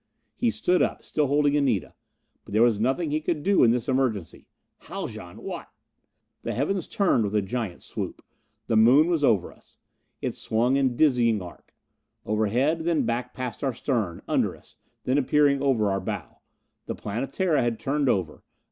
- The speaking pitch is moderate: No, low, 125 Hz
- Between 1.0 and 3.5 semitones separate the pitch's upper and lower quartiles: No, average, 5.1 semitones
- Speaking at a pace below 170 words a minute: No, average, 175 wpm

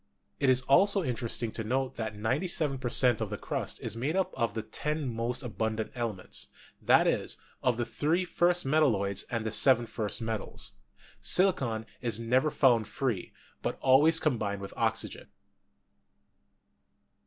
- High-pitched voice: No, low, 120 Hz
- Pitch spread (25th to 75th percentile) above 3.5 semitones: Yes, average, 4.0 semitones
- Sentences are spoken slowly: No, average, 155 wpm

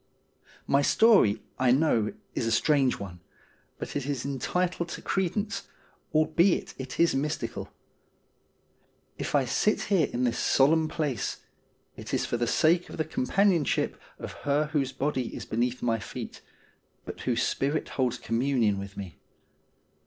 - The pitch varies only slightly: No, average, 4.7 semitones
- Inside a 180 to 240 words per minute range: No, average, 145 wpm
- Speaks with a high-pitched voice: No, medium, 140 Hz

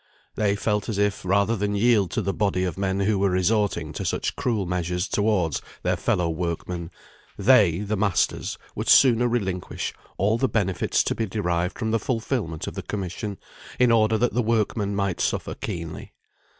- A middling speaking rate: Yes, average, 175 wpm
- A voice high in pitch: No, low, 100 Hz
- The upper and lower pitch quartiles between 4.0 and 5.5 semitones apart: No, average, 3.4 semitones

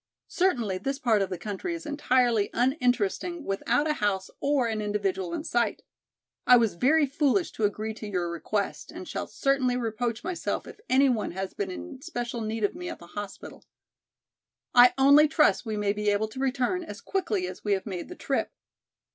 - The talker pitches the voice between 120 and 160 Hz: No, high, 240 Hz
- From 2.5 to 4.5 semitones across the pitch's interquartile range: No, wide, 5.5 semitones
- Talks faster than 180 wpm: Yes, average, 190 wpm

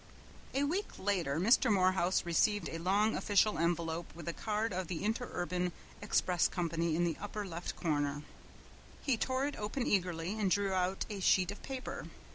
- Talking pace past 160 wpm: Yes, average, 170 wpm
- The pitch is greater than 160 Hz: Yes, medium, 185 Hz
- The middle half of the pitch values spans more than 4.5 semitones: No, average, 3.6 semitones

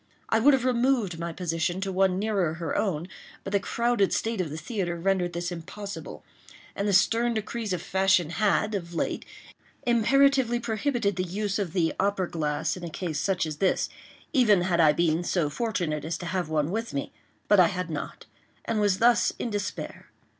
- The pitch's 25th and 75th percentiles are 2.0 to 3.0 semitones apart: No, average, 4.2 semitones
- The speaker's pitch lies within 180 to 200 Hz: Yes, high, 190 Hz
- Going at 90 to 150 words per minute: No, average, 185 wpm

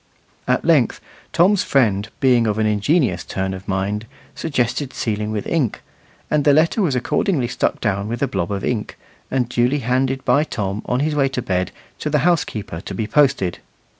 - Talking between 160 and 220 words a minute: Yes, average, 185 wpm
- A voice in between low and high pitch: No, low, 120 Hz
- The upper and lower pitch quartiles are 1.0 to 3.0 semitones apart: No, wide, 5.4 semitones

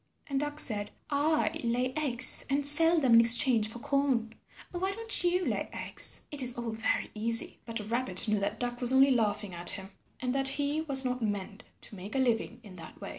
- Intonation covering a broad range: No, average, 4.3 semitones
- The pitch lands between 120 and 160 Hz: No, high, 245 Hz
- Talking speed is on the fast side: Yes, fast, 210 wpm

